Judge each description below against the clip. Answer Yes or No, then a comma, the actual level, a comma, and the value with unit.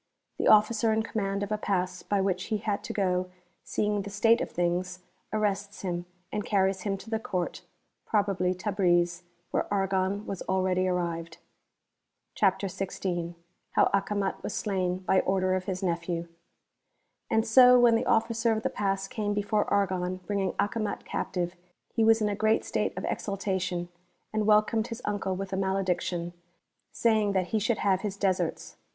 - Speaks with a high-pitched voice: Yes, high, 195 Hz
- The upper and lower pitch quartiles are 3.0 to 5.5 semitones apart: No, narrow, 2.5 semitones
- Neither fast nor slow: Yes, average, 170 wpm